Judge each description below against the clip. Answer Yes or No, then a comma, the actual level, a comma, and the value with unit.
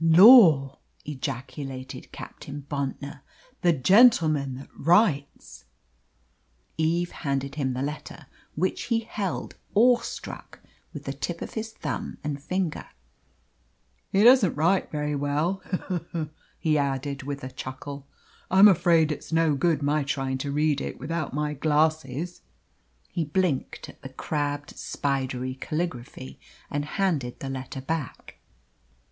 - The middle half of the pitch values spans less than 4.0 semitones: Yes, average, 3.6 semitones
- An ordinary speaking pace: No, slow, 130 wpm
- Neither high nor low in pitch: Yes, medium, 150 Hz